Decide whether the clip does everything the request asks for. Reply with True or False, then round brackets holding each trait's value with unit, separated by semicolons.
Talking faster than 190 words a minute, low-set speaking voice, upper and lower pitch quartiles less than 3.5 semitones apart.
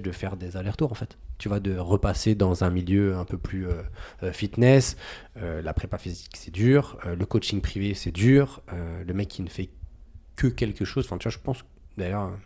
True (215 wpm; 95 Hz; 2.9 semitones)